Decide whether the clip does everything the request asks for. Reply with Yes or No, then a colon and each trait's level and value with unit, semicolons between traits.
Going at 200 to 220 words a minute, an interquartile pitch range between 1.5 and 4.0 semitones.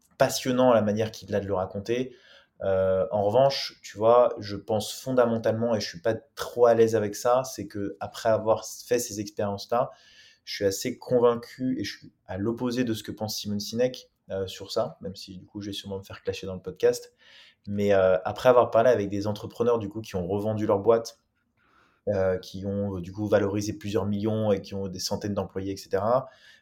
Yes: average, 215 wpm; average, 3.1 semitones